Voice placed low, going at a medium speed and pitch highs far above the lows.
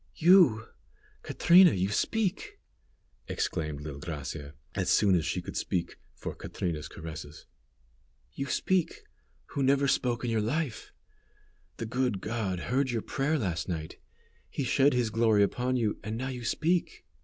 Yes: low, 115 Hz; average, 145 wpm; wide, 7.2 semitones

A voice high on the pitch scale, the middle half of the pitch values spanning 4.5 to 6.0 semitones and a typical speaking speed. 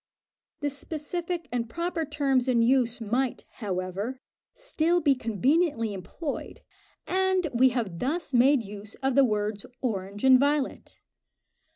No: very high, 260 Hz; average, 5.3 semitones; slow, 130 wpm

